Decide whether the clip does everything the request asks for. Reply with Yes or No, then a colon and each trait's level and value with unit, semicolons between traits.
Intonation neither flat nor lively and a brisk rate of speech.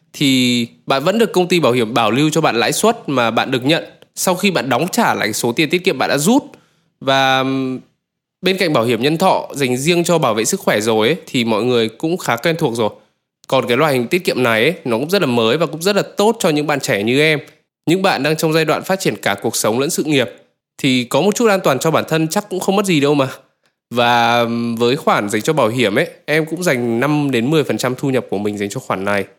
No: wide, 6.2 semitones; fast, 270 wpm